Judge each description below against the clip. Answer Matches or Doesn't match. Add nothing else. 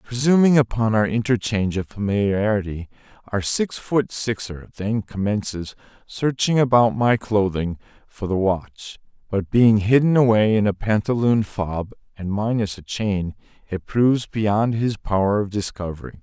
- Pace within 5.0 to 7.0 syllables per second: Doesn't match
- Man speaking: Matches